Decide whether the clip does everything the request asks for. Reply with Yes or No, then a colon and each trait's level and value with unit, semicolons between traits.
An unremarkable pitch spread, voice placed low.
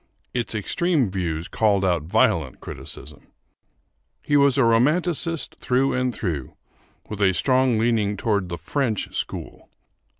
No: wide, 6.0 semitones; low, 110 Hz